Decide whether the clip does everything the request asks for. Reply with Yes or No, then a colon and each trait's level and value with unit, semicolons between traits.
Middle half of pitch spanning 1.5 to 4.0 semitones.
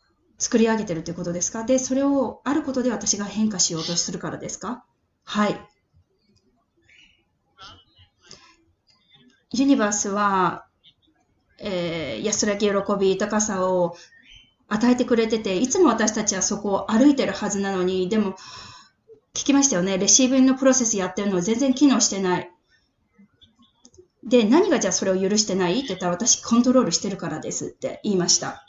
No: average, 5.1 semitones